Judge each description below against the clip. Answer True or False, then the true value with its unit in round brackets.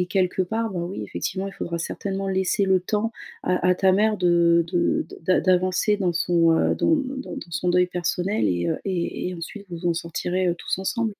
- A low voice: False (180 Hz)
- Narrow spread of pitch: True (2.1 semitones)